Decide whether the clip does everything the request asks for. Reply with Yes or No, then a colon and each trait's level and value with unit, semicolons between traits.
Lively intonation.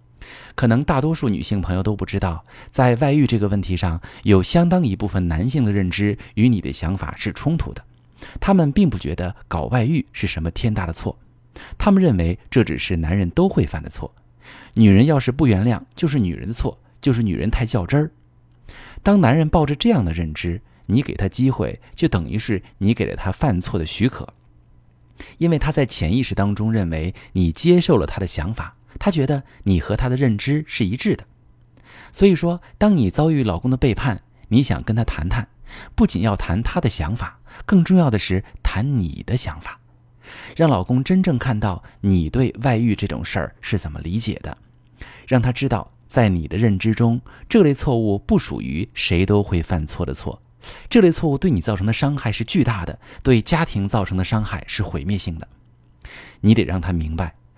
Yes: wide, 5.9 semitones